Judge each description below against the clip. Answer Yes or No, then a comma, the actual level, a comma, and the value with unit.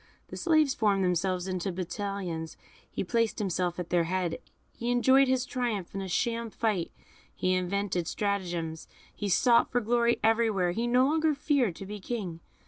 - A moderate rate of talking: Yes, average, 170 wpm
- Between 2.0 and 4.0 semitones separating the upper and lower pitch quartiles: No, average, 4.9 semitones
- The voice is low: No, high, 200 Hz